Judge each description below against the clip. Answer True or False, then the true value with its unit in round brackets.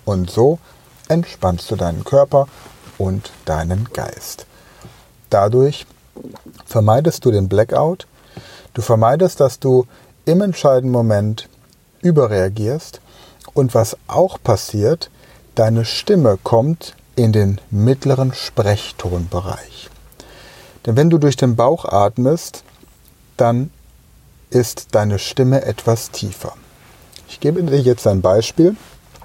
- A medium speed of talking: False (105 wpm)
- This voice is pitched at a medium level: False (120 Hz)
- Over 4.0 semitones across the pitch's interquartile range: True (4.5 semitones)